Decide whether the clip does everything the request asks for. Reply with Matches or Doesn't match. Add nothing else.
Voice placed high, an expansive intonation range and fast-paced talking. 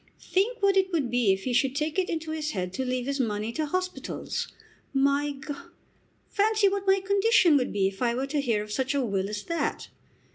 Matches